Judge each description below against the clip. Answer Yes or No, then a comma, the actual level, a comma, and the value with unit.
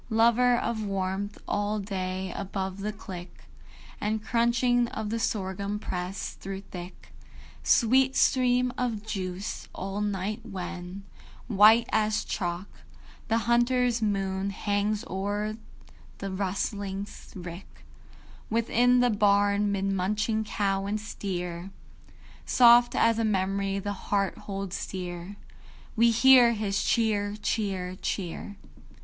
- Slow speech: Yes, slow, 115 wpm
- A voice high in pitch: Yes, high, 205 Hz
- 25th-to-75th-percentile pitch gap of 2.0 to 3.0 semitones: Yes, narrow, 2.6 semitones